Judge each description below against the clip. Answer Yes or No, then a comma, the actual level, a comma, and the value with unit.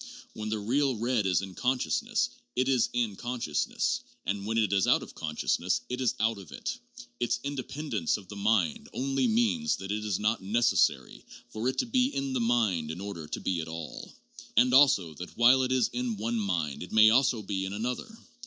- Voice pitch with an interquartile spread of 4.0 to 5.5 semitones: Yes, average, 4.8 semitones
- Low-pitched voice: Yes, low, 110 Hz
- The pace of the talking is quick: Yes, fast, 210 wpm